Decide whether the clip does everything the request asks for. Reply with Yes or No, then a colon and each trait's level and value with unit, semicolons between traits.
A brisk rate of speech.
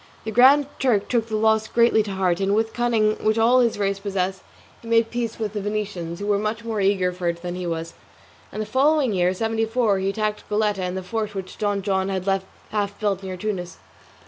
Yes: fast, 235 wpm